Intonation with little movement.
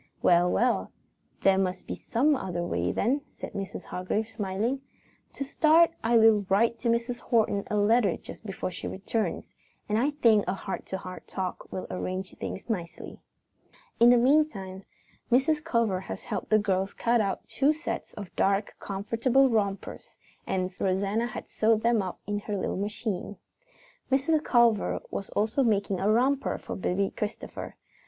No: average, 3.7 semitones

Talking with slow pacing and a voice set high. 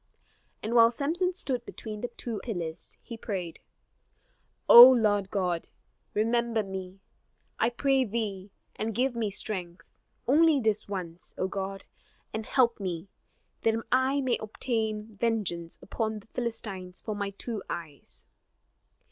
Yes: slow, 130 wpm; high, 215 Hz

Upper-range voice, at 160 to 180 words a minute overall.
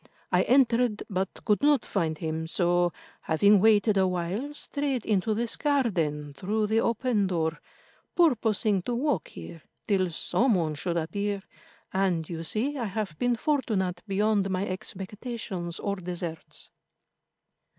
No: high, 200 Hz; average, 140 wpm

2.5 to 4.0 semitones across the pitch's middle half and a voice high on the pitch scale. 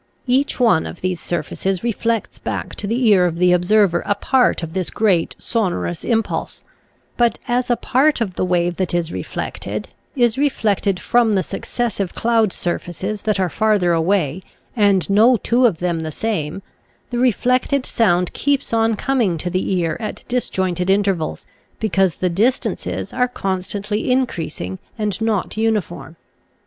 No: average, 4.6 semitones; high, 200 Hz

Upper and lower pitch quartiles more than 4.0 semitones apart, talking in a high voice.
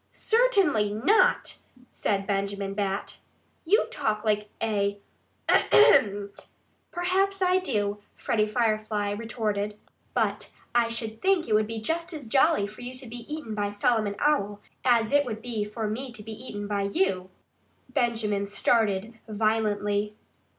No: average, 3.3 semitones; high, 215 Hz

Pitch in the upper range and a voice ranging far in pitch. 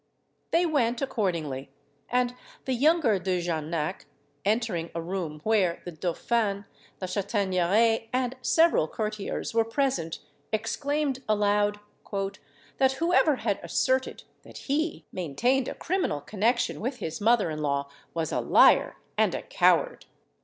Yes: high, 215 Hz; wide, 6.5 semitones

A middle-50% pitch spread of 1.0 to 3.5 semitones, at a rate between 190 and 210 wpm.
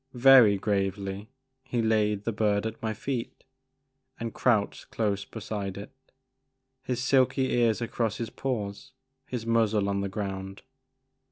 No: average, 2.7 semitones; slow, 135 wpm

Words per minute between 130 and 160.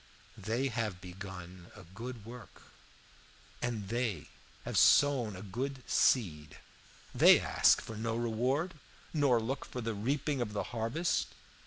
Yes: slow, 135 wpm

